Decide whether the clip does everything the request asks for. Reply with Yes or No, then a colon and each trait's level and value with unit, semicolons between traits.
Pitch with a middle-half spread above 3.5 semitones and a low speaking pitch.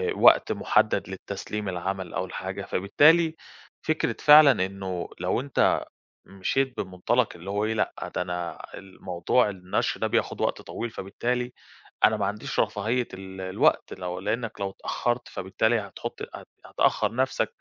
Yes: average, 4.4 semitones; low, 100 Hz